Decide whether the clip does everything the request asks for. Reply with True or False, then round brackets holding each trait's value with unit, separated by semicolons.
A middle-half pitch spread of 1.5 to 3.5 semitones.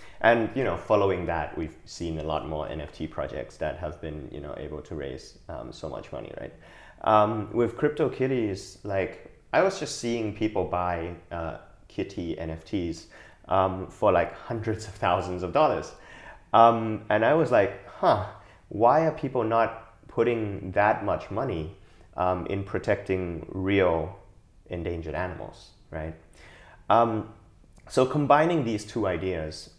False (4.8 semitones)